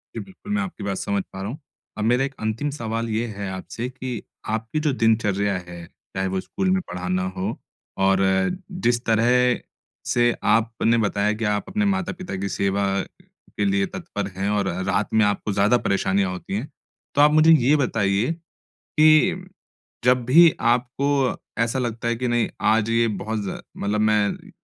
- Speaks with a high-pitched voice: No, low, 115 Hz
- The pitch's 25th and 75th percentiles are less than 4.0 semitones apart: No, average, 4.3 semitones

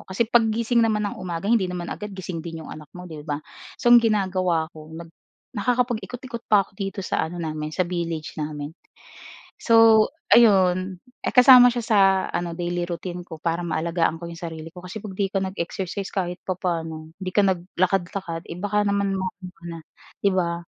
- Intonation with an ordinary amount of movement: Yes, average, 3.6 semitones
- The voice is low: No, medium, 185 Hz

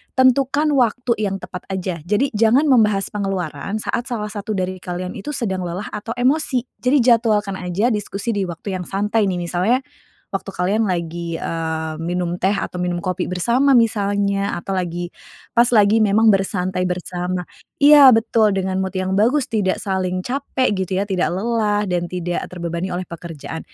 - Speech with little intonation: No, average, 3.8 semitones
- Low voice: No, high, 195 Hz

